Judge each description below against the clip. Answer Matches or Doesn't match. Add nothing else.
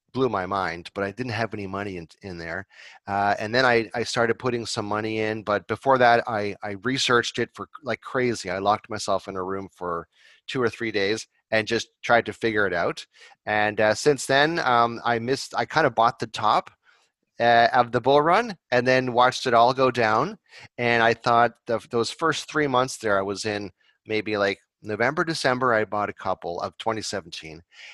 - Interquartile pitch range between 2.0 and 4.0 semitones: Matches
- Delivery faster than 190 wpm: Matches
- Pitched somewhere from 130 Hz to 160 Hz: Doesn't match